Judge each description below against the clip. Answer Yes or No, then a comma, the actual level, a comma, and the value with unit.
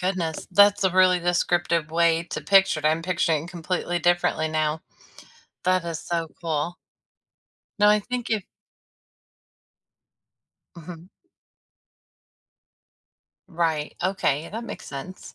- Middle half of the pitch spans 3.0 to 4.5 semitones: No, narrow, 2.5 semitones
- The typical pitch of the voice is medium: Yes, medium, 175 Hz